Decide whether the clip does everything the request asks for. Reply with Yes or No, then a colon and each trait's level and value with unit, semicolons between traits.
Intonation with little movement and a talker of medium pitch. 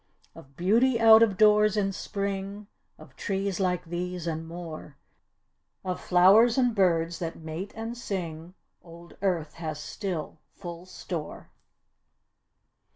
No: average, 3.5 semitones; medium, 180 Hz